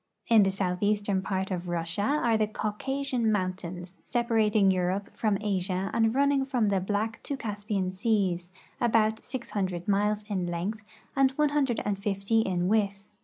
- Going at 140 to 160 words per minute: Yes, average, 145 wpm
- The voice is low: No, high, 205 Hz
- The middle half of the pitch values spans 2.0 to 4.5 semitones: Yes, average, 3.0 semitones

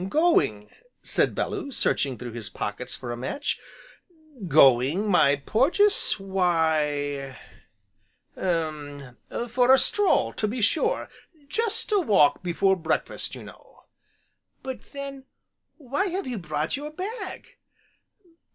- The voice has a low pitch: No, high, 190 Hz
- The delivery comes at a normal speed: No, slow, 115 wpm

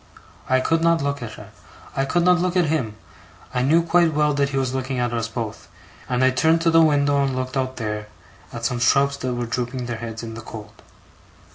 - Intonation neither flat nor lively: Yes, average, 4.1 semitones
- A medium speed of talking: No, fast, 230 wpm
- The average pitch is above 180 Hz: No, low, 130 Hz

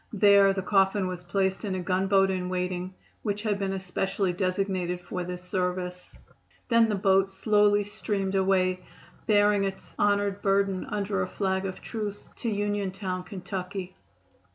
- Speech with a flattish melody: Yes, narrow, 1.7 semitones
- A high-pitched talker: Yes, high, 195 Hz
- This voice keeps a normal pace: Yes, average, 150 wpm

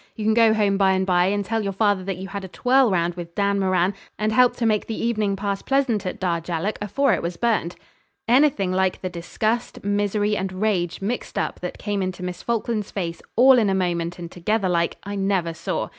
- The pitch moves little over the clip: No, average, 3.0 semitones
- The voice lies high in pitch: Yes, high, 200 Hz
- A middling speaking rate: No, fast, 220 wpm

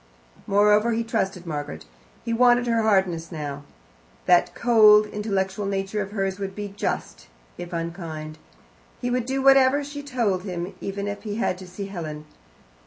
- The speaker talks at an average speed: Yes, average, 160 wpm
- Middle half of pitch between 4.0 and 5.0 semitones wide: Yes, average, 4.3 semitones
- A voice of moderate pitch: No, high, 200 Hz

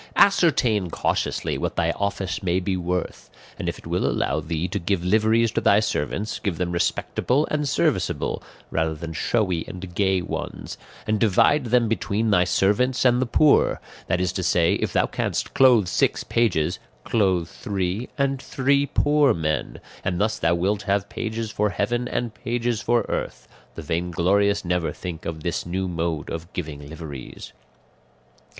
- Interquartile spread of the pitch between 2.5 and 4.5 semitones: No, average, 4.9 semitones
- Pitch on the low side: Yes, very low, 95 Hz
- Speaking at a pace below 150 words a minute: No, average, 165 wpm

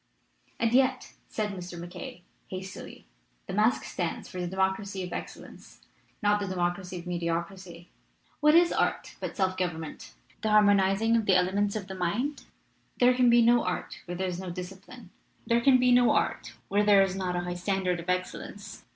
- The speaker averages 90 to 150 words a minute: No, average, 185 wpm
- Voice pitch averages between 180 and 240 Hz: Yes, high, 190 Hz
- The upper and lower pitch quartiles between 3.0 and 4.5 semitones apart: Yes, average, 3.4 semitones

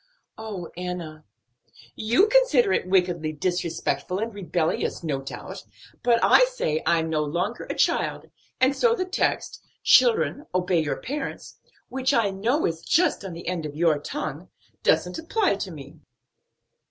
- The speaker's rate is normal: Yes, average, 150 wpm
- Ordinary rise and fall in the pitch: No, wide, 9.0 semitones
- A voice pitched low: No, medium, 185 Hz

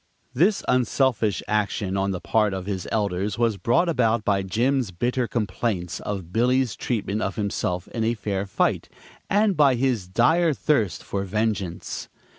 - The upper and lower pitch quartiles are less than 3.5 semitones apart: No, average, 4.4 semitones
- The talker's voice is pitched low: Yes, low, 110 Hz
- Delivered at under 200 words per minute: Yes, average, 155 wpm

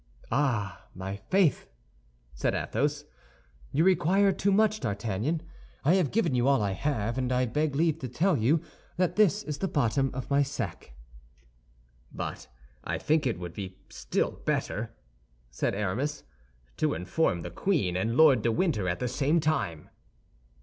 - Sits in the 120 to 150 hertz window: Yes, low, 135 Hz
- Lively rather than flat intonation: Yes, wide, 7.7 semitones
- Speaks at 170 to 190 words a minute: No, average, 155 wpm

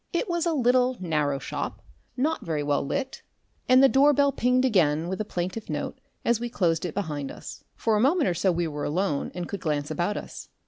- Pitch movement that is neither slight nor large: No, wide, 8.0 semitones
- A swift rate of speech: Yes, fast, 220 wpm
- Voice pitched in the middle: No, high, 200 Hz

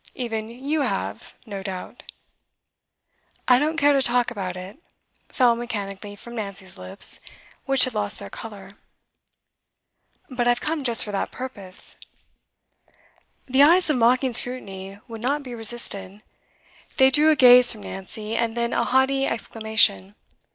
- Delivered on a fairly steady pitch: No, average, 4.3 semitones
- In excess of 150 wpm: No, average, 145 wpm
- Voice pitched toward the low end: No, high, 235 Hz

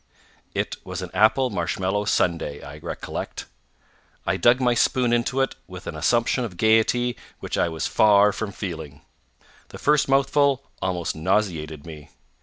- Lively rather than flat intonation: Yes, wide, 6.5 semitones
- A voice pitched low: Yes, low, 105 Hz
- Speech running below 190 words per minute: Yes, average, 150 wpm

